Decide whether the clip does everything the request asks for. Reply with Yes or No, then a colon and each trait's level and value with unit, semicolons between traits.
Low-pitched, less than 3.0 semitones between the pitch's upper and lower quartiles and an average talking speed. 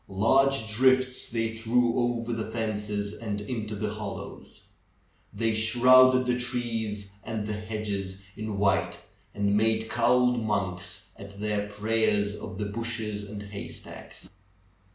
No: low, 110 Hz; narrow, 2.4 semitones; slow, 130 wpm